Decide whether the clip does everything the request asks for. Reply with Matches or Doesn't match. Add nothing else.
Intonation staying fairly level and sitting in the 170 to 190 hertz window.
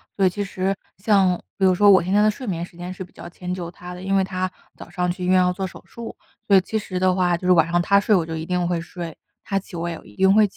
Matches